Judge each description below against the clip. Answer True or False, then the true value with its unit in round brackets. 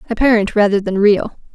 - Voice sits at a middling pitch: False (210 Hz)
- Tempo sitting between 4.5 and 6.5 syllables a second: True (5.7 syllables/s)